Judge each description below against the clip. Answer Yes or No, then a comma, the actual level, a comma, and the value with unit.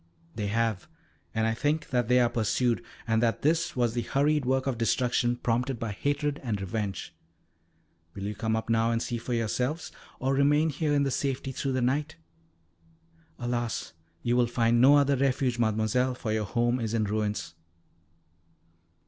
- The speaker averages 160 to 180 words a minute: Yes, average, 170 wpm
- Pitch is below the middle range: Yes, low, 120 Hz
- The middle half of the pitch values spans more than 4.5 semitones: No, average, 3.1 semitones